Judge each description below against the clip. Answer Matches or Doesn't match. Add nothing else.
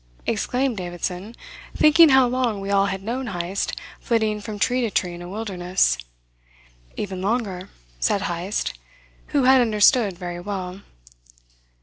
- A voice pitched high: Matches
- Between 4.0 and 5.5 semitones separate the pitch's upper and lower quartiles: Matches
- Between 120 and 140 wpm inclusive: Matches